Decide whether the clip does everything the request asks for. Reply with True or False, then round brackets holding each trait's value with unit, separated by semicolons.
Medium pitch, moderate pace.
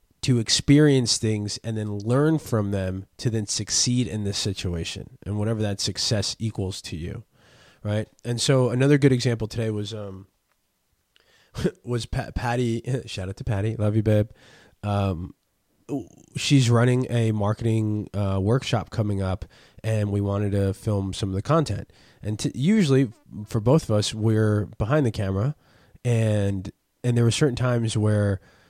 False (110 Hz; 160 wpm)